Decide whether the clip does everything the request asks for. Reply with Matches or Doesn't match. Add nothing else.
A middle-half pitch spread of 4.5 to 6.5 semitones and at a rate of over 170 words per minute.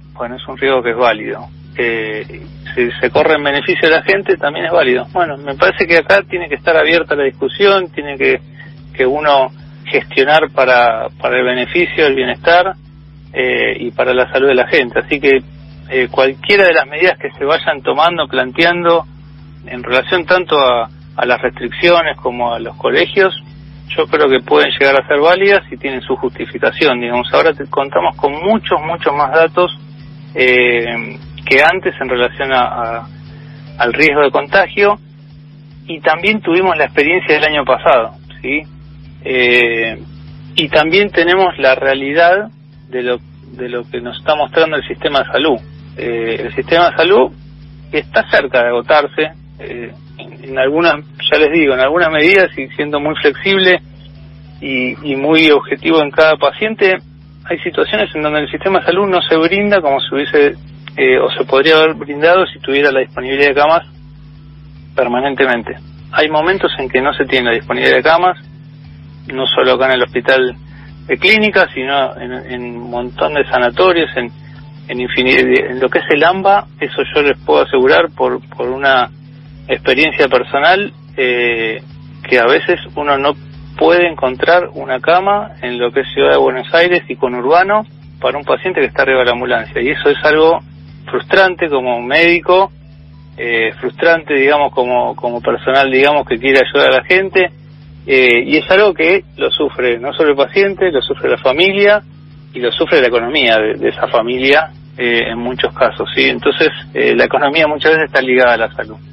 Matches